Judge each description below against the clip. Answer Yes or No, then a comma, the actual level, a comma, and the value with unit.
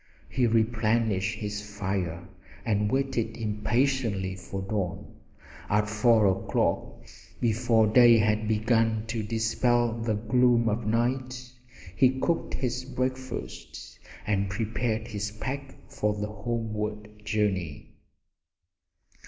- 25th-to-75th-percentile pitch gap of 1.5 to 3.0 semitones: Yes, narrow, 2.4 semitones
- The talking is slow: Yes, slow, 105 wpm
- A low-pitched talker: Yes, low, 110 Hz